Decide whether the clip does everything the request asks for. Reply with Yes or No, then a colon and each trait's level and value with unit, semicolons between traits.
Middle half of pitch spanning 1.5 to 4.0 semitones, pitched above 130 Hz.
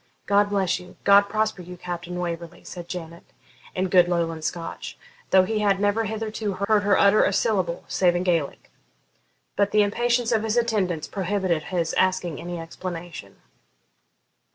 Yes: average, 2.9 semitones; medium, 185 Hz